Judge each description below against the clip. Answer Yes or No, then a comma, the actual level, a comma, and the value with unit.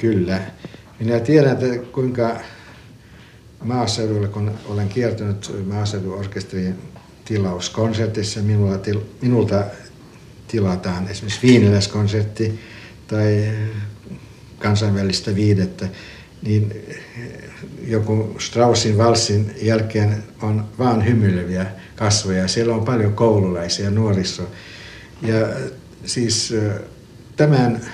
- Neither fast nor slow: No, slow, 80 wpm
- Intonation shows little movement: Yes, narrow, 2.3 semitones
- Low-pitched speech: Yes, low, 110 Hz